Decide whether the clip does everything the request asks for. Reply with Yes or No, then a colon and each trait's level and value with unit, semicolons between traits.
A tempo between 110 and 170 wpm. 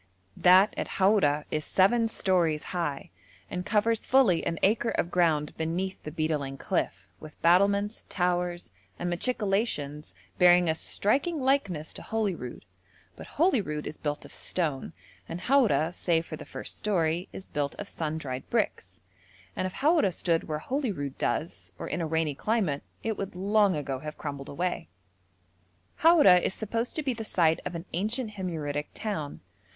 Yes: average, 160 wpm